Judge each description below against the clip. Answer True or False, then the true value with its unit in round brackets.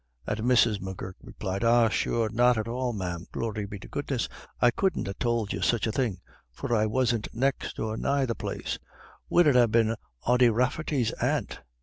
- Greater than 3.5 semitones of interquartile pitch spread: False (2.7 semitones)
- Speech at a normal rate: True (190 wpm)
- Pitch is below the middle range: True (115 Hz)